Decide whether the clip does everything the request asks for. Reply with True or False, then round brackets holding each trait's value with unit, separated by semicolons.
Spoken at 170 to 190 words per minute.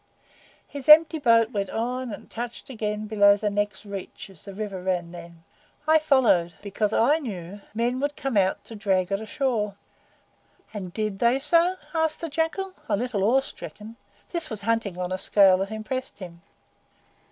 True (175 wpm)